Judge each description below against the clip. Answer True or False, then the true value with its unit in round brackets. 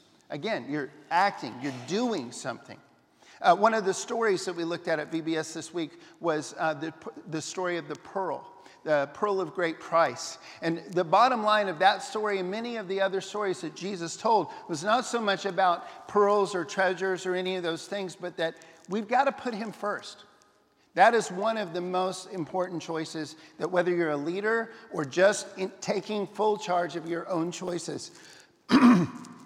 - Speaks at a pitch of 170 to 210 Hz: True (185 Hz)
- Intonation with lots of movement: False (3.8 semitones)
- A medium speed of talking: True (185 wpm)